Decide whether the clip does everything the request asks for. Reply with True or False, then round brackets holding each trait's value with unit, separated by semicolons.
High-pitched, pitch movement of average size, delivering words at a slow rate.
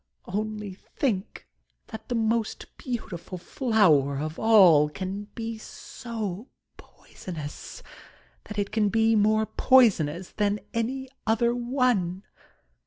True (215 Hz; 3.7 semitones; 110 wpm)